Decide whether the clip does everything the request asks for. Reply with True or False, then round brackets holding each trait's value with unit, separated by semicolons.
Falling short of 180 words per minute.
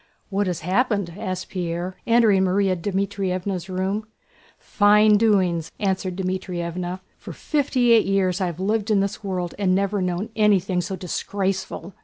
True (145 wpm)